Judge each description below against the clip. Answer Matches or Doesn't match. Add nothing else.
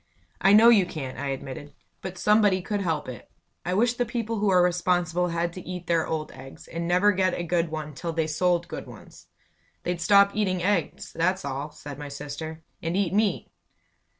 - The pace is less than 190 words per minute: Doesn't match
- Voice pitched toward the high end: Doesn't match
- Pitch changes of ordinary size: Matches